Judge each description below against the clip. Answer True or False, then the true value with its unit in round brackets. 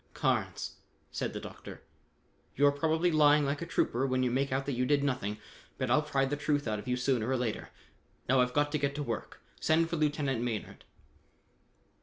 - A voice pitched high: False (140 Hz)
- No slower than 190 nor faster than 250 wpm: True (200 wpm)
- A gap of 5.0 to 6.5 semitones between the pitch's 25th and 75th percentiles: False (2.8 semitones)